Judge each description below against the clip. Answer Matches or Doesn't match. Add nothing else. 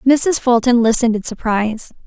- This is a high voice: Matches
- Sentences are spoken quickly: Doesn't match